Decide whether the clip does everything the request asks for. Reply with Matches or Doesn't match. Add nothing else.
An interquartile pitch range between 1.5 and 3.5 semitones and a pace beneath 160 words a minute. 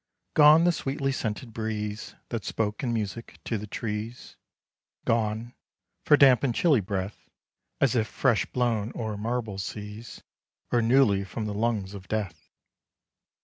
Matches